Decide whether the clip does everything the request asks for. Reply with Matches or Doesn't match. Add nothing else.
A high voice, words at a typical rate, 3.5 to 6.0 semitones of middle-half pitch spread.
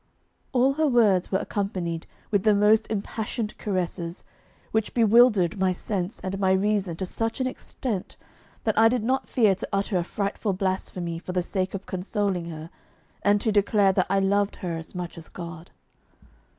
Doesn't match